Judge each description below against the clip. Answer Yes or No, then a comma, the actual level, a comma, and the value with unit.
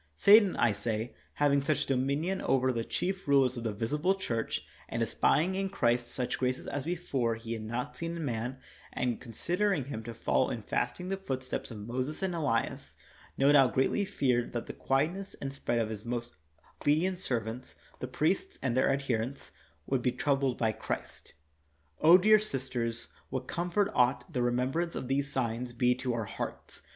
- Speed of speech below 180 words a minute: No, average, 185 wpm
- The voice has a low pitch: Yes, low, 130 Hz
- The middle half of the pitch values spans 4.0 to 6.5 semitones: Yes, average, 4.7 semitones